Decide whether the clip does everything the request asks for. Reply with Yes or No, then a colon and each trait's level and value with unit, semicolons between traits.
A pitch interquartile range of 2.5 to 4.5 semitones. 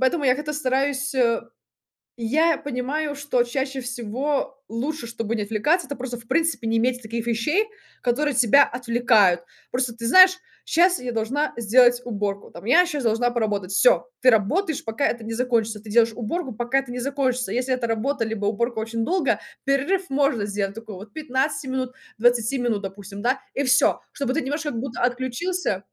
Yes: average, 3.7 semitones